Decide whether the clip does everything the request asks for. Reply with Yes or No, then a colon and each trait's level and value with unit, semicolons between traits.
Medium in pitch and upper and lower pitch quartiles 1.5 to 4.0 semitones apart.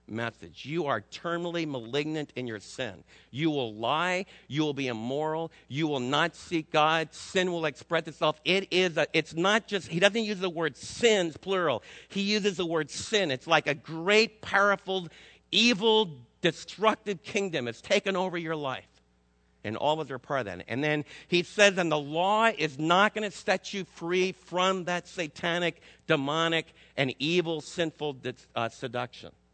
No: medium, 160 Hz; average, 4.8 semitones